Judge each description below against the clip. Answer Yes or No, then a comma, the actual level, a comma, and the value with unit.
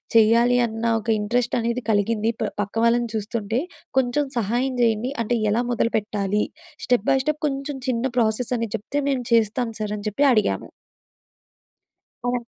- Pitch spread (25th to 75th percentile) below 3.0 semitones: Yes, narrow, 2.4 semitones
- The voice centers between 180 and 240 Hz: Yes, high, 230 Hz